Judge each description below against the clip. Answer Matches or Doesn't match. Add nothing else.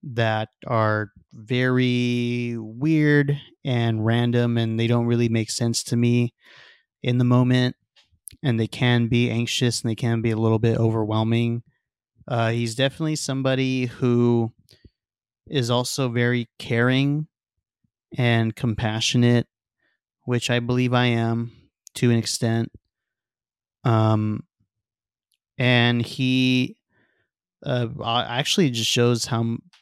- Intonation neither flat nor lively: Doesn't match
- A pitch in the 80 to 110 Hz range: Doesn't match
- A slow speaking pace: Matches